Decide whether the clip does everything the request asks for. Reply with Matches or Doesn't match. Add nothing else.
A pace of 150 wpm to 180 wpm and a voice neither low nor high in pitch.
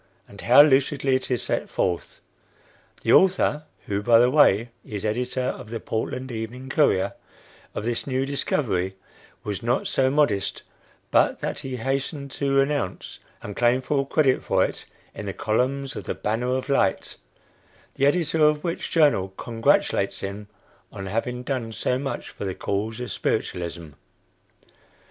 Doesn't match